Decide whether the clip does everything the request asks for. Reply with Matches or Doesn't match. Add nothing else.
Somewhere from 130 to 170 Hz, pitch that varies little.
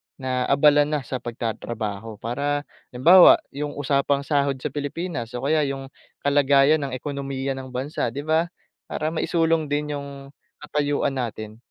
Matches